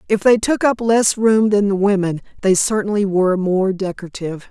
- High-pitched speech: Yes, high, 200 Hz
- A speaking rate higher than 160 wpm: Yes, average, 185 wpm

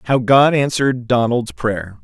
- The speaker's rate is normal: Yes, average, 150 wpm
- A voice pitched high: No, low, 125 Hz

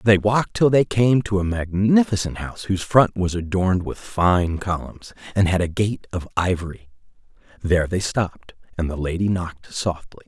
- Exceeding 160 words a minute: Yes, average, 175 wpm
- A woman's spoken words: No, male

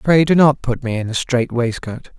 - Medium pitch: No, low, 130 Hz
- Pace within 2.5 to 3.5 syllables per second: No, 4.9 syllables/s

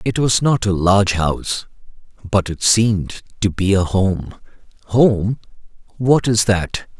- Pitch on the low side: Yes, low, 100 Hz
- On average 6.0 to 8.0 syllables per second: No, 4.0 syllables/s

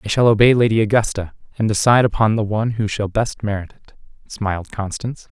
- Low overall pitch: Yes, low, 110 Hz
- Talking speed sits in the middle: Yes, average, 190 wpm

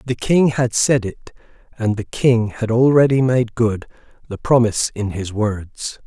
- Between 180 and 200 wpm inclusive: No, average, 170 wpm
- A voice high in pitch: No, low, 115 Hz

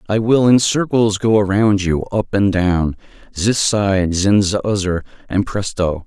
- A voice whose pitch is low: Yes, low, 100 Hz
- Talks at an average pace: Yes, average, 170 wpm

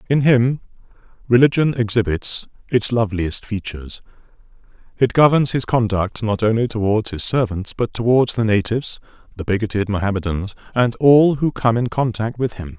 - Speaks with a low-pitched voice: Yes, low, 115 Hz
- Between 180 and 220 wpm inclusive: No, average, 145 wpm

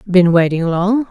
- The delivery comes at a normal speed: Yes, average, 165 wpm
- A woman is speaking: Yes, female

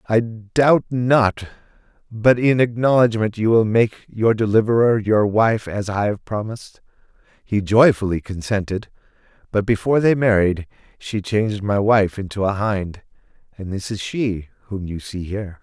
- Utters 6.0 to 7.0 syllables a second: No, 4.5 syllables/s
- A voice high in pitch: No, low, 105 Hz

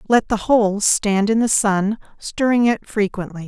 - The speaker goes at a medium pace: Yes, average, 175 wpm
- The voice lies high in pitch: Yes, high, 210 Hz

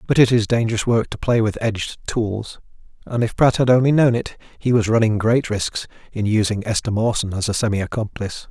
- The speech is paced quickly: Yes, fast, 210 wpm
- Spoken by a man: Yes, male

